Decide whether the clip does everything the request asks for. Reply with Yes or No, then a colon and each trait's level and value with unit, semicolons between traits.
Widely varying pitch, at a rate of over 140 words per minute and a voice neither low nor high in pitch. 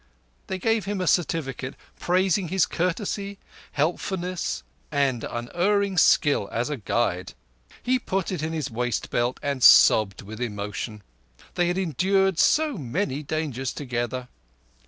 No: wide, 7.4 semitones; slow, 135 wpm; medium, 155 Hz